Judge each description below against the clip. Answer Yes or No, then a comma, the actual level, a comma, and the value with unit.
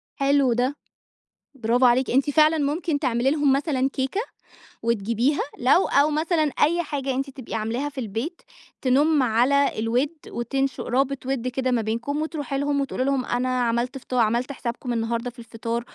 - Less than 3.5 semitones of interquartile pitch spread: Yes, average, 3.0 semitones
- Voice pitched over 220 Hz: Yes, very high, 260 Hz